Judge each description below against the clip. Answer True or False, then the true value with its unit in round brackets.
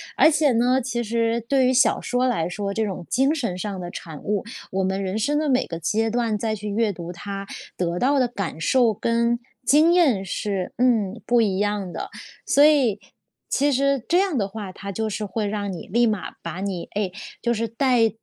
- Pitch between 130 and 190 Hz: False (220 Hz)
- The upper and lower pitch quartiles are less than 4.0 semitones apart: False (4.3 semitones)